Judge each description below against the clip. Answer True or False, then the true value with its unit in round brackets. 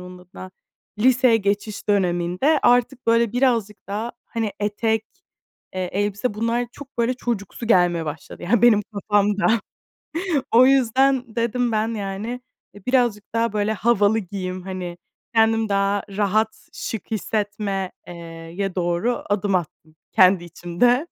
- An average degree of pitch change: True (3.3 semitones)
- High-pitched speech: True (210 Hz)